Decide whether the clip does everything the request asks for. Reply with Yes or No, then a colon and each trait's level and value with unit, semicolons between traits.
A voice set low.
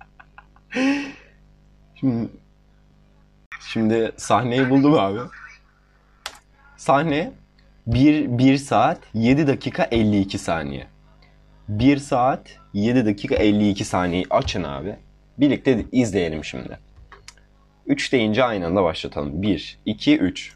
Yes: low, 120 Hz